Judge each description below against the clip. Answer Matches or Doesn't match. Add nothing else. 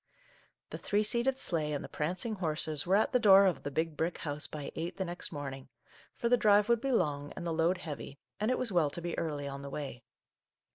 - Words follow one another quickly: Matches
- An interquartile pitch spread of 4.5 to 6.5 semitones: Matches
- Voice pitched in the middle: Matches